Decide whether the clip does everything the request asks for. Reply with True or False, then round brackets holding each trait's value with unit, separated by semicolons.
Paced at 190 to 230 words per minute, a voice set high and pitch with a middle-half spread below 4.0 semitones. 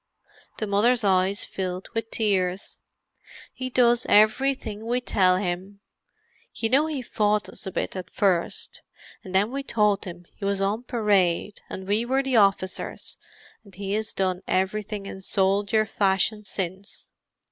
False (145 wpm; 205 Hz; 2.9 semitones)